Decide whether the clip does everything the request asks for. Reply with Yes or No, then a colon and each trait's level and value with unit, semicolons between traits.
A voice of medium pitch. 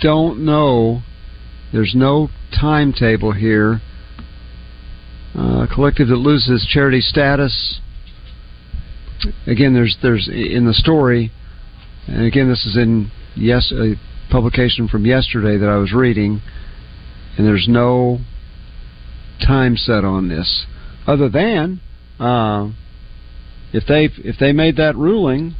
No: low, 115 Hz